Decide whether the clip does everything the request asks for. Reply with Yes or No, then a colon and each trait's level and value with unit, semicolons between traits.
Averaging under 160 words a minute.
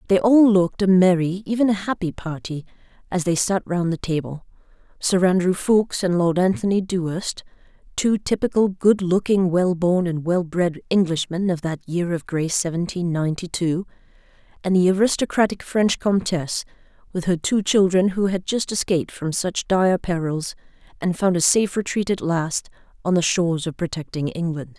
No: average, 170 wpm